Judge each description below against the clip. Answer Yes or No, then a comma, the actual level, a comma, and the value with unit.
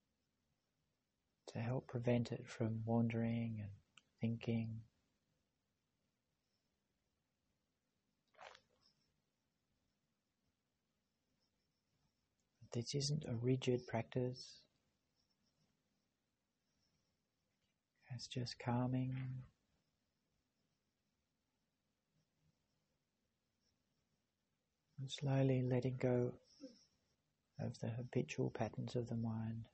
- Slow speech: Yes, slow, 55 wpm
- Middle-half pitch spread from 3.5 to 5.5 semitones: No, narrow, 1.9 semitones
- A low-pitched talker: Yes, low, 125 Hz